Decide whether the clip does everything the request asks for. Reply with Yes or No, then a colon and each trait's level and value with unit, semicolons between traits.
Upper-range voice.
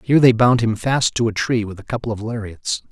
No: low, 115 Hz